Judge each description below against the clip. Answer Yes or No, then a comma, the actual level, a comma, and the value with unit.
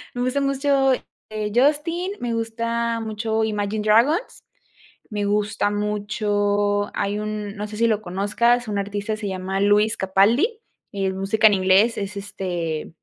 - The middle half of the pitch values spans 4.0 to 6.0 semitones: No, narrow, 2.4 semitones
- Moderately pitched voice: No, high, 210 Hz